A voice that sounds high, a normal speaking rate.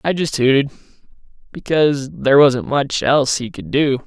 No: medium, 140 Hz; average, 160 wpm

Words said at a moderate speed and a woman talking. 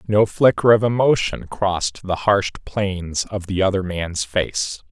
No: average, 160 wpm; male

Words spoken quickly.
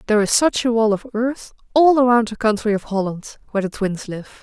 Yes: fast, 230 wpm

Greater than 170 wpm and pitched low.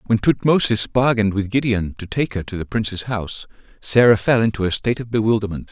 Yes: average, 200 wpm; low, 110 Hz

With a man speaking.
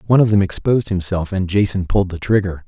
Yes: male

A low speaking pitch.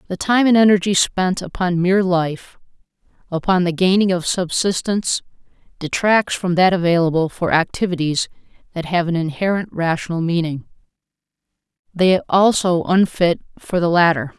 No: medium, 180 Hz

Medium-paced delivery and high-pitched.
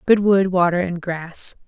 No: average, 180 wpm; medium, 180 Hz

